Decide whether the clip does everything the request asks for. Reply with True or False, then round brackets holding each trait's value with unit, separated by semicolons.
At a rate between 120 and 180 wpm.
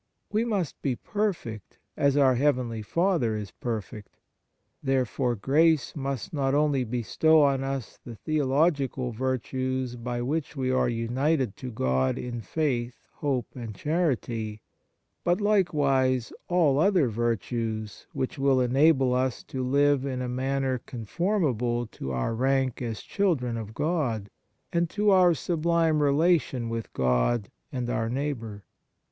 True (135 wpm)